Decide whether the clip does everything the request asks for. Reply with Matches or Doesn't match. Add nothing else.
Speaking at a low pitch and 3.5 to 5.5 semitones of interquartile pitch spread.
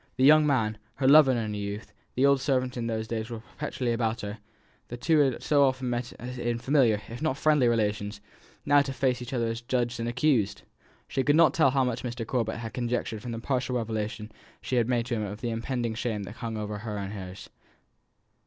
Doesn't match